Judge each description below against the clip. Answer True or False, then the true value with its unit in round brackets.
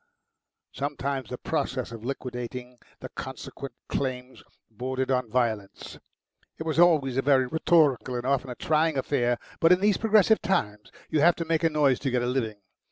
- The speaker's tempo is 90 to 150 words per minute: False (170 wpm)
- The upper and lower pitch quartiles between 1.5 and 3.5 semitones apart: False (4.2 semitones)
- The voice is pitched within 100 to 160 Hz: True (135 Hz)